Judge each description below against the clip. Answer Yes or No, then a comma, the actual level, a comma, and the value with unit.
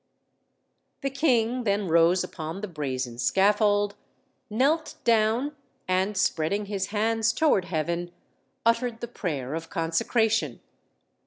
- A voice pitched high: Yes, high, 205 Hz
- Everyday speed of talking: No, slow, 110 wpm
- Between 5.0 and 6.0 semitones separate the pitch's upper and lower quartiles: Yes, average, 5.3 semitones